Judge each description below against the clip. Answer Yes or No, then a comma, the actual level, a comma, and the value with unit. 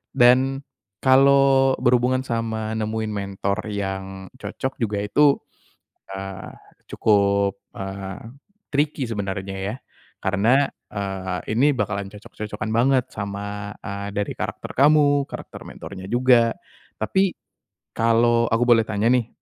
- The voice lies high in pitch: No, low, 110 Hz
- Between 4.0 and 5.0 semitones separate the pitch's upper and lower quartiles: Yes, average, 4.3 semitones